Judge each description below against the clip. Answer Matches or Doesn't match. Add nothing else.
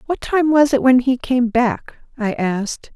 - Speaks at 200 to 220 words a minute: Matches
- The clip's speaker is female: Matches